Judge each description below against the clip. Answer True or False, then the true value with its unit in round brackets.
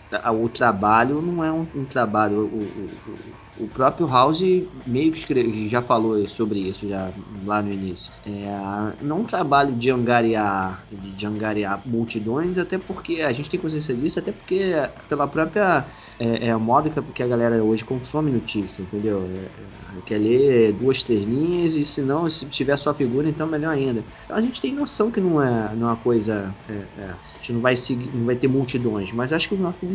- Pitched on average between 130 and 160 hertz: False (120 Hz)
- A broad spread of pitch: True (5.8 semitones)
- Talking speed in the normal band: False (200 wpm)